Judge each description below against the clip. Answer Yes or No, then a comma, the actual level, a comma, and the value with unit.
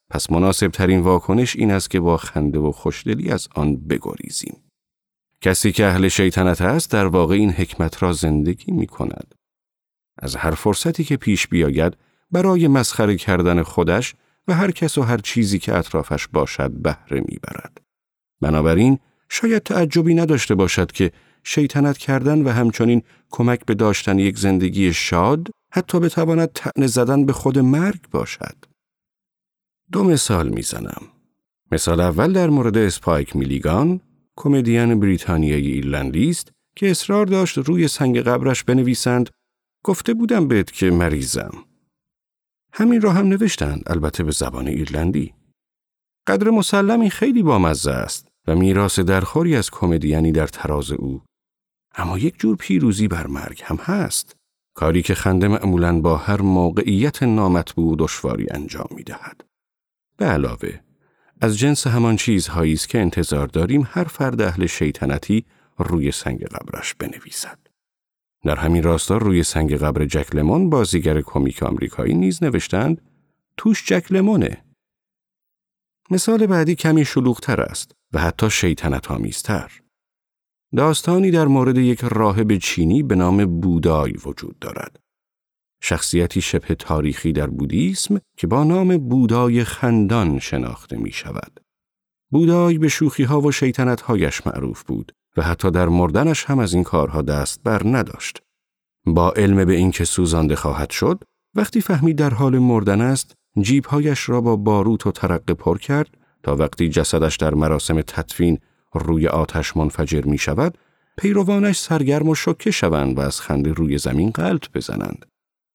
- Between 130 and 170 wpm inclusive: Yes, average, 140 wpm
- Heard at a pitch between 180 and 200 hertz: No, low, 100 Hz